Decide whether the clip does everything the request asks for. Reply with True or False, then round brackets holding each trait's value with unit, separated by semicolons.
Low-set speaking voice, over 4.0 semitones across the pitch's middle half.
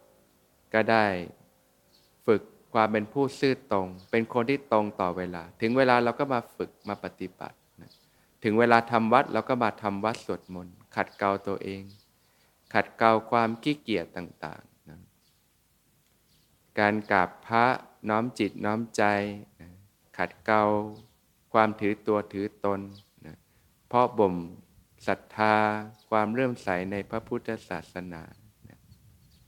False (105 Hz; 3.4 semitones)